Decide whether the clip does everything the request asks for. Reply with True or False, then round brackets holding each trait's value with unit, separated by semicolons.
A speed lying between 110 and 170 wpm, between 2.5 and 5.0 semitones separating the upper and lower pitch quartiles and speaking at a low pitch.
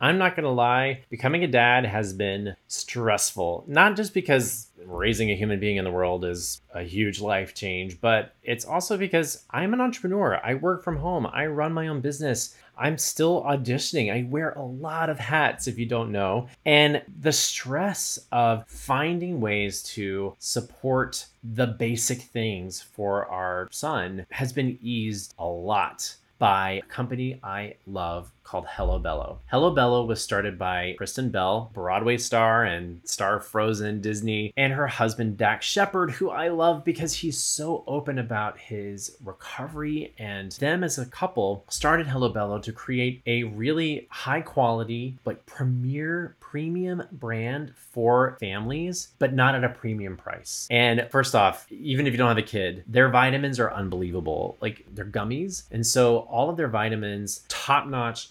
False (165 wpm; 5.6 semitones; 120 Hz)